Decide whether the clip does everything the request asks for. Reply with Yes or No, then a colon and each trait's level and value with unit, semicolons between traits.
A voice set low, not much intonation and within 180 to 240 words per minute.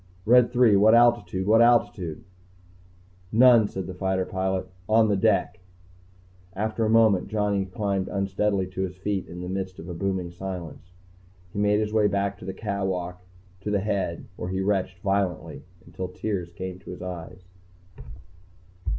No: very low, 95 Hz; narrow, 2.2 semitones; average, 165 wpm